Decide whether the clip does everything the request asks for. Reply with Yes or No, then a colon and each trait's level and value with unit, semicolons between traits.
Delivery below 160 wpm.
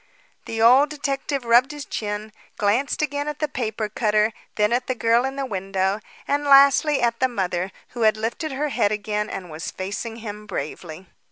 No: average, 185 wpm